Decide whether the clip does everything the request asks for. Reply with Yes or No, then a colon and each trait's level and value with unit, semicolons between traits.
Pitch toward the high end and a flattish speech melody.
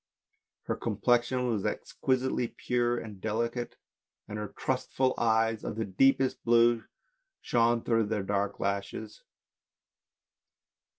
No: low, 115 Hz; narrow, 2.3 semitones